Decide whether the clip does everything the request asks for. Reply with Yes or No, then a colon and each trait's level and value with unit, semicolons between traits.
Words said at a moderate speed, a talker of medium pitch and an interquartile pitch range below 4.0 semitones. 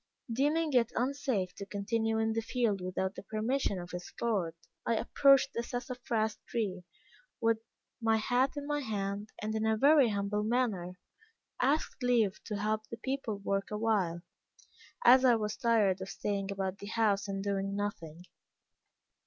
No: average, 160 wpm; high, 215 Hz; average, 3.5 semitones